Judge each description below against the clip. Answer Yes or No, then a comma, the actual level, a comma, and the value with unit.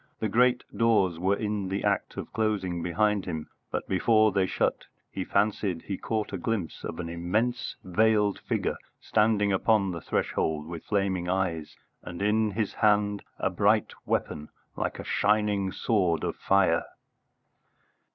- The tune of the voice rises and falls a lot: No, average, 3.2 semitones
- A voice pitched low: Yes, low, 100 Hz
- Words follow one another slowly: No, average, 150 wpm